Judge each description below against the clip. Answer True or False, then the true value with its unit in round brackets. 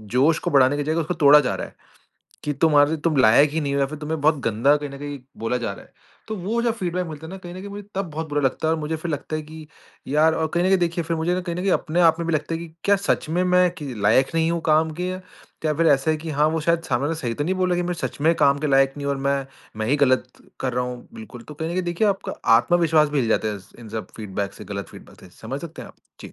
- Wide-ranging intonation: False (3.5 semitones)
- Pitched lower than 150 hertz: False (155 Hz)